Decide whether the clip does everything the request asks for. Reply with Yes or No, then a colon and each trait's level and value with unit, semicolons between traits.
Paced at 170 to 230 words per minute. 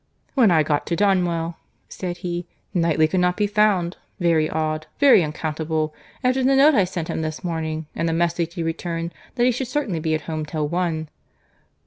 Yes: average, 190 wpm